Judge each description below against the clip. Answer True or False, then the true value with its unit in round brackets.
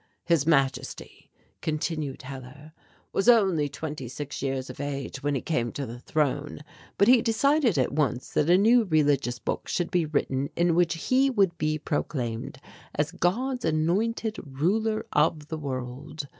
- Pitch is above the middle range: False (155 Hz)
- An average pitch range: True (4.7 semitones)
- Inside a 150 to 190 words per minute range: True (155 wpm)